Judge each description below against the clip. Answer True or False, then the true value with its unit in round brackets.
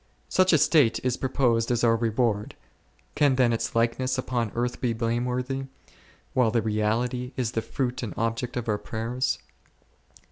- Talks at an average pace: True (155 wpm)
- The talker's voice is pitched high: False (120 Hz)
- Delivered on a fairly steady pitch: True (1.9 semitones)